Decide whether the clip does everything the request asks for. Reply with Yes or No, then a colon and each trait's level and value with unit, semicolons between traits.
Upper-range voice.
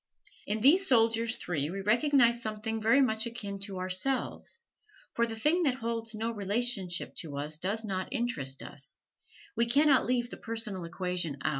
Yes: high, 225 Hz